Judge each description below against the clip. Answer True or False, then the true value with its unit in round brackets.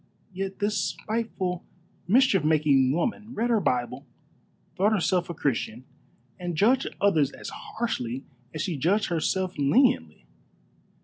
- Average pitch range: False (6.6 semitones)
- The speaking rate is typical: False (125 wpm)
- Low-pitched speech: False (180 Hz)